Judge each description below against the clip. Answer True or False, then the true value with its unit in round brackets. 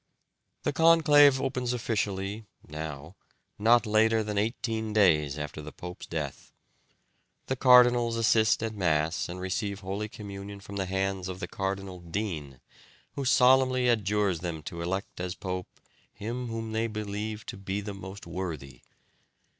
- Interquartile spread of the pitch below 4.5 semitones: True (3.7 semitones)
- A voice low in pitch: True (100 Hz)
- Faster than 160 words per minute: False (145 wpm)